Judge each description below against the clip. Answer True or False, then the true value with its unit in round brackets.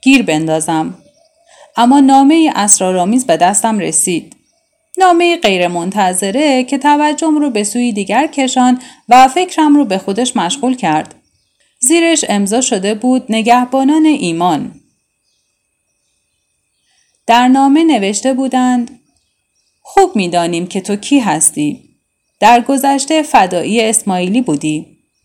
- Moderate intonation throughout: False (6.3 semitones)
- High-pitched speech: True (250 Hz)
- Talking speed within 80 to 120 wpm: True (110 wpm)